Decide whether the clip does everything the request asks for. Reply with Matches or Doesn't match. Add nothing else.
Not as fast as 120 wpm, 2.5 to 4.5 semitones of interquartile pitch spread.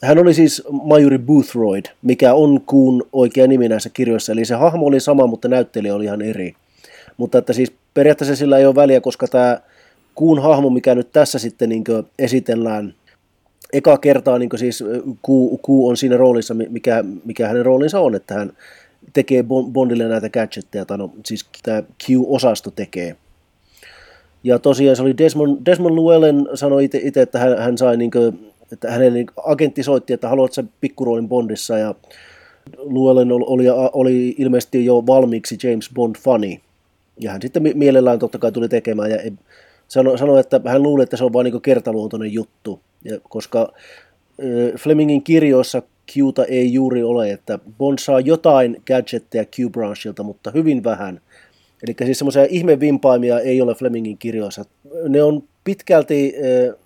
Doesn't match